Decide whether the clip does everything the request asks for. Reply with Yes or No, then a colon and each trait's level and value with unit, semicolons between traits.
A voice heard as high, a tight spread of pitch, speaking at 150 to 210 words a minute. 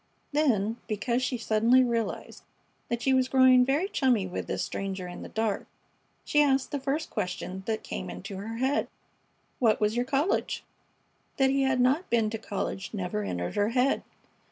No: high, 235 Hz; average, 4.2 semitones; average, 175 wpm